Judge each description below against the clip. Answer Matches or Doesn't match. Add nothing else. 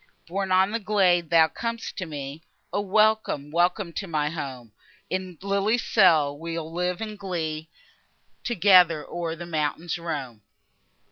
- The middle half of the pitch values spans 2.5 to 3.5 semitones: Doesn't match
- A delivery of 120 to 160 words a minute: Matches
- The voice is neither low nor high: Matches